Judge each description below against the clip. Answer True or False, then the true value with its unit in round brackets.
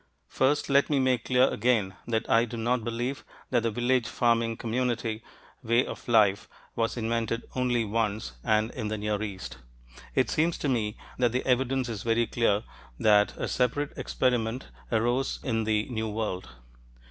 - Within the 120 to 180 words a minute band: True (165 wpm)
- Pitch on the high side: False (115 Hz)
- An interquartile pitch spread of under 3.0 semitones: True (2.5 semitones)